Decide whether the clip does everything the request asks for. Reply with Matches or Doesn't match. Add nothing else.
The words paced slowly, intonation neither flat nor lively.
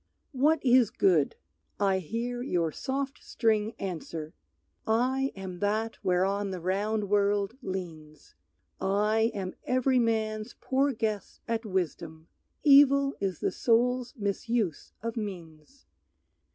Matches